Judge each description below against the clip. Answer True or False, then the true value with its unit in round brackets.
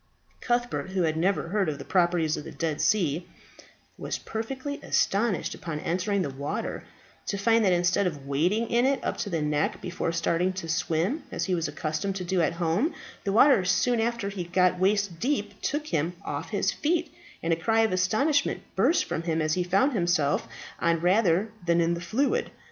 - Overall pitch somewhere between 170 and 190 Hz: True (185 Hz)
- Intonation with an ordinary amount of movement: True (4.9 semitones)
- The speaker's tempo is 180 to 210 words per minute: True (195 wpm)